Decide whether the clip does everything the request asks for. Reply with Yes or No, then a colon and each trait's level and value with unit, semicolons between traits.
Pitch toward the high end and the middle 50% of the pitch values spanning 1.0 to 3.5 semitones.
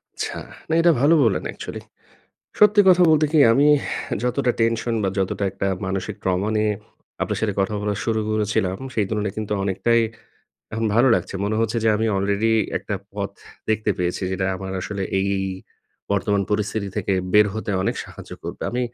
No: low, 105 Hz; narrow, 2.6 semitones